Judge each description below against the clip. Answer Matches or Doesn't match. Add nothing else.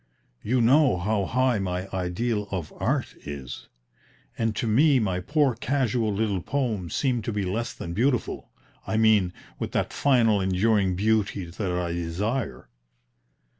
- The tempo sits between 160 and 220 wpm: Doesn't match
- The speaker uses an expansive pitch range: Doesn't match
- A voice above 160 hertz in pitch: Doesn't match